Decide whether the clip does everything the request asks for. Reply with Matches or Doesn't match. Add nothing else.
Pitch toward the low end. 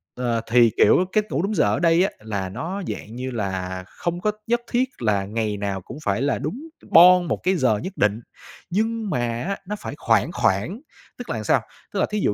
Matches